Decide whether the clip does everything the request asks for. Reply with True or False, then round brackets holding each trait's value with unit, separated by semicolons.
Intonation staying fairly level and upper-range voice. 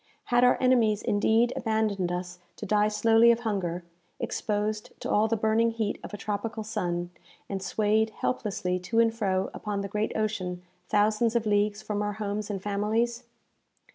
True (1.8 semitones; 210 Hz)